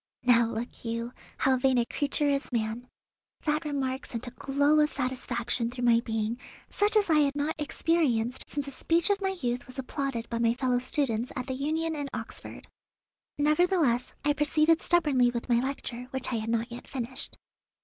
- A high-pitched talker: Yes, very high, 260 Hz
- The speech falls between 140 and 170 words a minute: No, average, 185 wpm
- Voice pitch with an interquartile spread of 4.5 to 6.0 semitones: No, average, 3.8 semitones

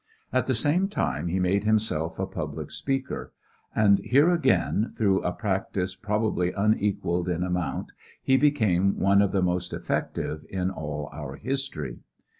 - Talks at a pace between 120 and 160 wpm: Yes, average, 150 wpm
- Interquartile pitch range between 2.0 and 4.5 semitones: Yes, average, 3.7 semitones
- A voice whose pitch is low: Yes, very low, 95 Hz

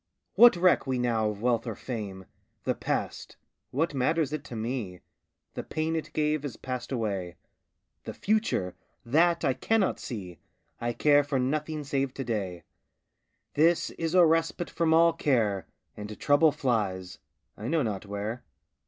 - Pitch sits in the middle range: No, low, 130 Hz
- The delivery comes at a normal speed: Yes, average, 155 wpm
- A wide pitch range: Yes, wide, 6.5 semitones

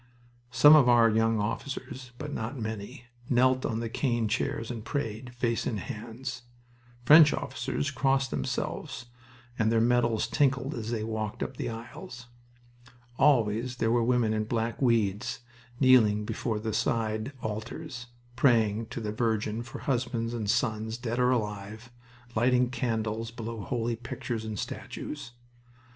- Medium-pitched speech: No, low, 115 Hz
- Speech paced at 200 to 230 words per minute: No, average, 145 wpm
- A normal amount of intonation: No, narrow, 2.3 semitones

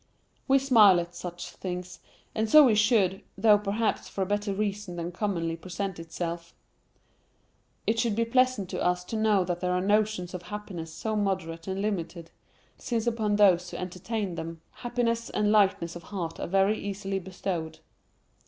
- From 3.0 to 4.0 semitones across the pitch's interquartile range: Yes, average, 3.4 semitones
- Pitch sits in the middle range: No, high, 195 Hz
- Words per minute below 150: No, average, 170 wpm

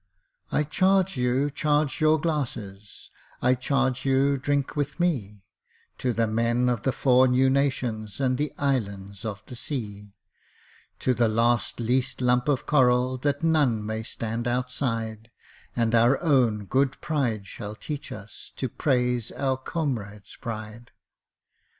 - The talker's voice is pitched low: Yes, low, 125 Hz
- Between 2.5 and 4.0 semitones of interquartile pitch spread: Yes, average, 3.7 semitones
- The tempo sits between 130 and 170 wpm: Yes, average, 140 wpm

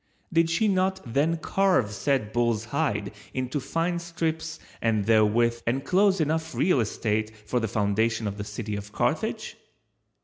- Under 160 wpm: Yes, average, 145 wpm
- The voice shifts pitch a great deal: Yes, wide, 7.3 semitones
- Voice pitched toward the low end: Yes, low, 120 Hz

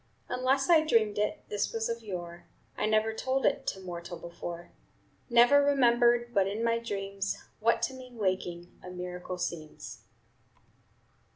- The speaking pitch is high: Yes, high, 215 Hz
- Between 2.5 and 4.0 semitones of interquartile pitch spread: No, average, 4.8 semitones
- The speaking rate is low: No, average, 150 wpm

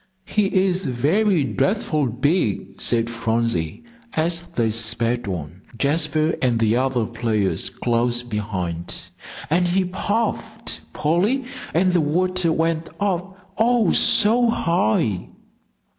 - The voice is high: No, medium, 150 Hz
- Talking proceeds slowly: Yes, slow, 115 wpm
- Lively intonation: Yes, wide, 8.1 semitones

